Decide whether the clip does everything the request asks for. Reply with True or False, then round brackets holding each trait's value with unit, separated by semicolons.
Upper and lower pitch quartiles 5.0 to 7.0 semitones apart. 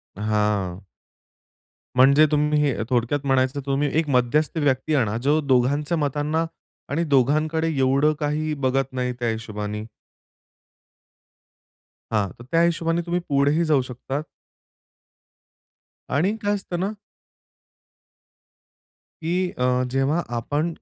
False (3.6 semitones)